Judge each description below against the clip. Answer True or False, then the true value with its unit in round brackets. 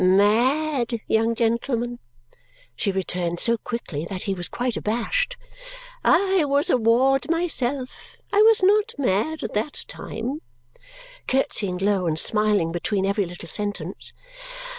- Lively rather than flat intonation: True (6.1 semitones)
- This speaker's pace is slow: True (130 wpm)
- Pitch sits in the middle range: False (230 Hz)